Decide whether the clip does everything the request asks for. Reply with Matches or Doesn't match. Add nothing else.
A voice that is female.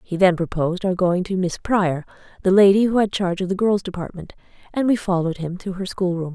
Matches